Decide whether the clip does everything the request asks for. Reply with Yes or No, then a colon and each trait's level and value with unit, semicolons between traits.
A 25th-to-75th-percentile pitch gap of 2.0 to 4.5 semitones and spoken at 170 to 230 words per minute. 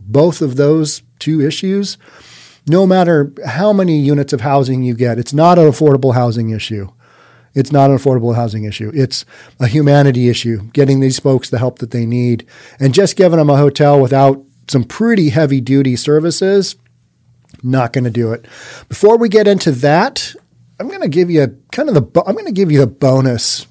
Yes: average, 4.1 semitones; average, 190 wpm